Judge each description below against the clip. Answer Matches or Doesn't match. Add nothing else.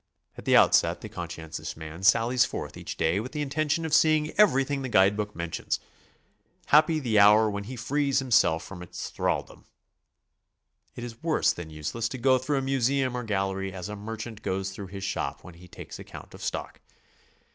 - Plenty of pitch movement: Matches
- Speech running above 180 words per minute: Matches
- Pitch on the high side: Doesn't match